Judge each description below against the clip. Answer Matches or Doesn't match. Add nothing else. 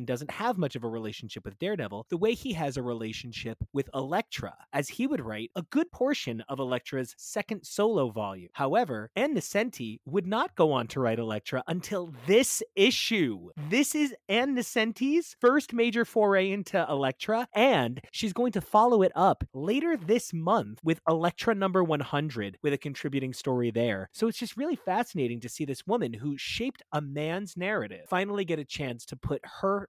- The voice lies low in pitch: Doesn't match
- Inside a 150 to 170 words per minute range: Doesn't match